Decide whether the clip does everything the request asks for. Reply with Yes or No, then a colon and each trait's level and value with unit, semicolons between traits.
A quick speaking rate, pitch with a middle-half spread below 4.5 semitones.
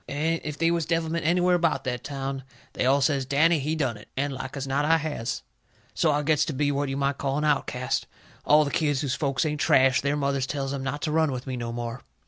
Yes: fast, 250 wpm; narrow, 2.5 semitones